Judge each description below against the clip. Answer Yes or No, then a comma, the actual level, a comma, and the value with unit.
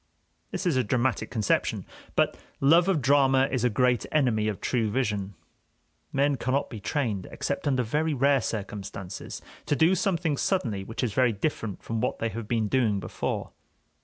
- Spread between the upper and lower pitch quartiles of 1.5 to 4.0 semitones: No, average, 4.7 semitones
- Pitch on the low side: Yes, low, 125 Hz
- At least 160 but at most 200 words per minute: Yes, average, 170 wpm